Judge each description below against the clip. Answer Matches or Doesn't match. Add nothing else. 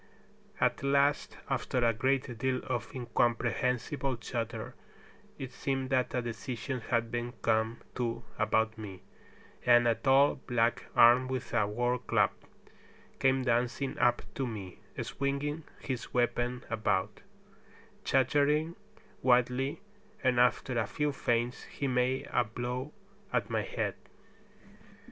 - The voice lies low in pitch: Matches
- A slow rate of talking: Matches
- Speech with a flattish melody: Matches